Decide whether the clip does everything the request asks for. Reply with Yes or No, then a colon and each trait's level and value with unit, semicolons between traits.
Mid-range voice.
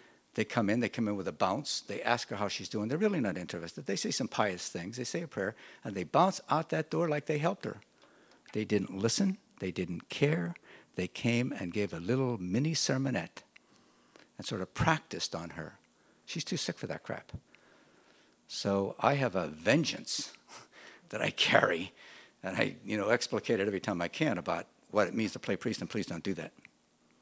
No: low, 105 Hz